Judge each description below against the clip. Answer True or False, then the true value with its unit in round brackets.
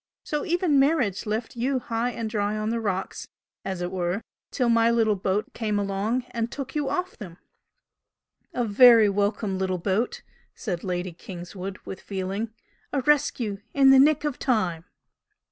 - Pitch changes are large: False (4.5 semitones)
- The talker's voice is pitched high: True (215 Hz)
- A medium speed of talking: True (160 wpm)